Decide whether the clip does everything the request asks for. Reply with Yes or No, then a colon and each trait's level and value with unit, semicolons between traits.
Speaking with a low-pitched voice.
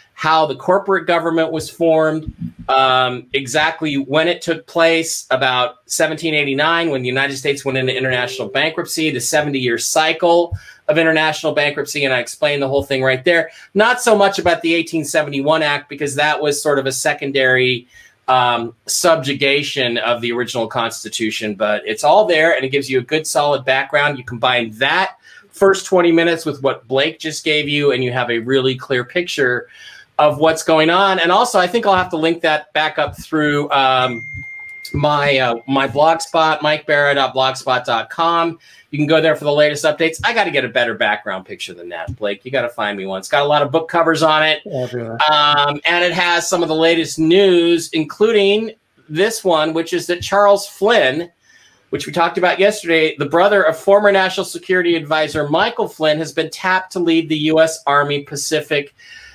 No: medium, 155 Hz